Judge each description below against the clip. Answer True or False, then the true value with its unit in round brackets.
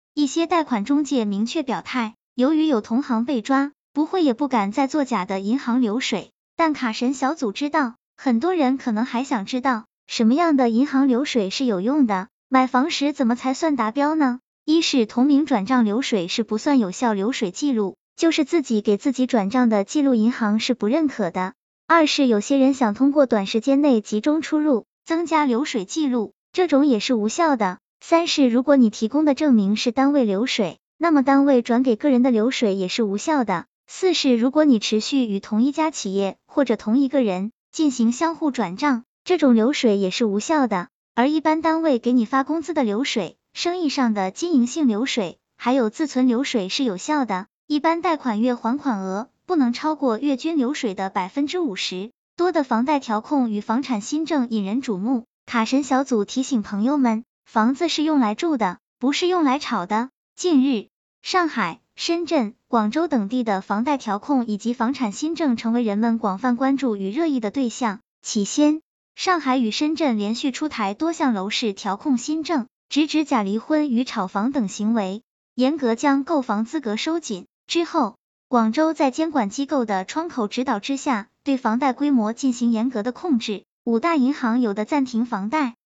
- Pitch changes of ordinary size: True (4.6 semitones)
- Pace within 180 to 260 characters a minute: False (280 characters per minute)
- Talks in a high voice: True (255 Hz)